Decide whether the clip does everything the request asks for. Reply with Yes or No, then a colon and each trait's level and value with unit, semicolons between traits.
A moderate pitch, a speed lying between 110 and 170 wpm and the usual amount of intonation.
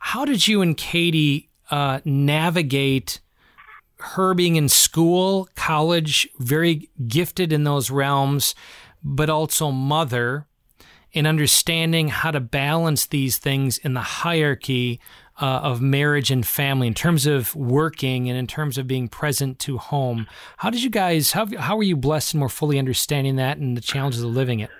Yes: medium, 145 Hz; average, 160 wpm; average, 3.3 semitones